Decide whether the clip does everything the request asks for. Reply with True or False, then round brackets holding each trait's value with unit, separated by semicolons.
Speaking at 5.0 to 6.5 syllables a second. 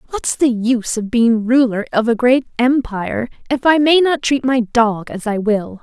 False (4.6 syllables/s)